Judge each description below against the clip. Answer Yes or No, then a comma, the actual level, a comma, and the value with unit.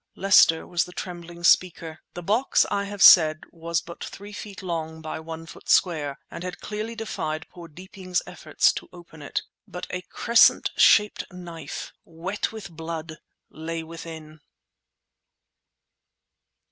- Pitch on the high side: No, medium, 170 Hz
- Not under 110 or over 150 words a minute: Yes, average, 140 wpm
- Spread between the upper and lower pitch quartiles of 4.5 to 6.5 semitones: No, average, 2.7 semitones